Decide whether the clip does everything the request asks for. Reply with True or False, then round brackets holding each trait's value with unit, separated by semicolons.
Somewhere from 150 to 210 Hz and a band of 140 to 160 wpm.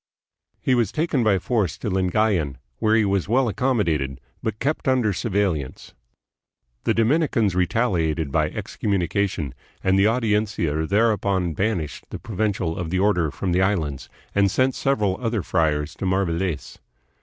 False (100 Hz; 145 wpm)